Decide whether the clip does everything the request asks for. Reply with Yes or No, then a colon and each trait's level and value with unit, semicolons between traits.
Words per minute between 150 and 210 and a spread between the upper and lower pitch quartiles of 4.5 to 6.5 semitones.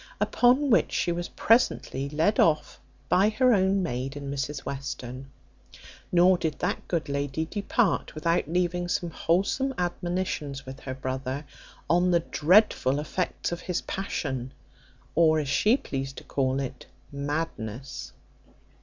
No: slow, 135 wpm; average, 4.8 semitones